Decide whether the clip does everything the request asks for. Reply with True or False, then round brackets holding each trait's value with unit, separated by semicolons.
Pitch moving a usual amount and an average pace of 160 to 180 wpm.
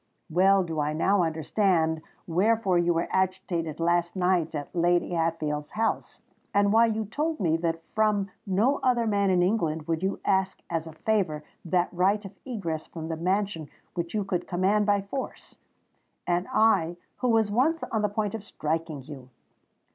True (4.0 semitones; 170 wpm)